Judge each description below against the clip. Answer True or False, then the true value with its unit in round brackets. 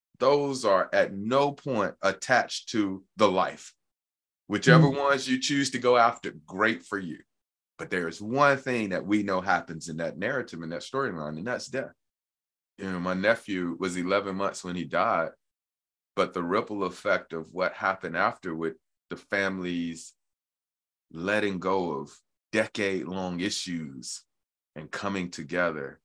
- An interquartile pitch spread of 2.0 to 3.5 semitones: False (4.0 semitones)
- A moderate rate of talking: True (150 wpm)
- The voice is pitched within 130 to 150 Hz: False (95 Hz)